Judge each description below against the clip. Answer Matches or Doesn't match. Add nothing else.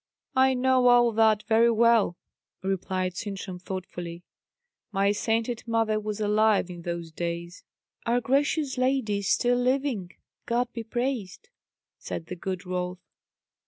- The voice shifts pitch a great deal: Doesn't match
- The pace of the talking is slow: Matches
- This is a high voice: Matches